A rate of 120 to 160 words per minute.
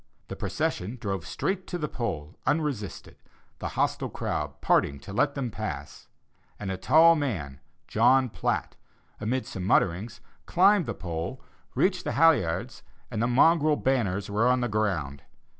Yes: average, 150 wpm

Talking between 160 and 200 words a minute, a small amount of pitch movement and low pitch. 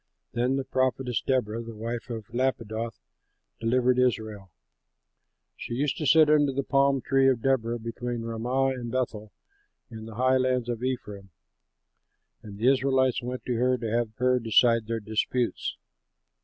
No: average, 150 wpm; narrow, 2.3 semitones; low, 125 Hz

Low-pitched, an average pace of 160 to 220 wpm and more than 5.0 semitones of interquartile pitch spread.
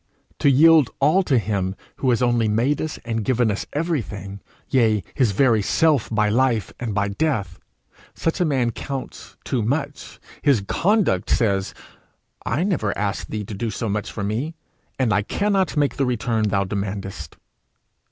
Yes: low, 115 Hz; average, 165 wpm; wide, 5.4 semitones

